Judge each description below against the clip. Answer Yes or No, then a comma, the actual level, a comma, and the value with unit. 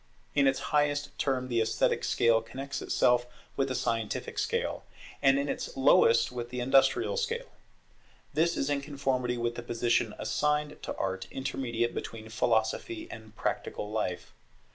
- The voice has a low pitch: Yes, low, 125 Hz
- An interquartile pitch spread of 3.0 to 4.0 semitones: Yes, average, 3.5 semitones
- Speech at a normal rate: Yes, average, 150 wpm